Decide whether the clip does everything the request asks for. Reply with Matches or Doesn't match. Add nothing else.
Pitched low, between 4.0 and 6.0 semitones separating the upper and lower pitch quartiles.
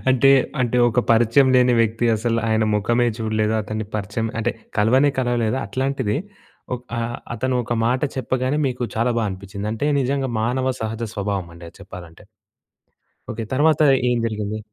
Doesn't match